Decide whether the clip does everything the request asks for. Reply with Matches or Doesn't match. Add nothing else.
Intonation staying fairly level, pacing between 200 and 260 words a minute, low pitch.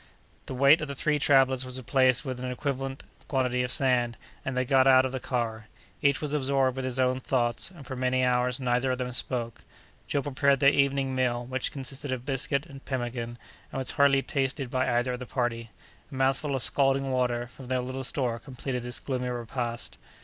Matches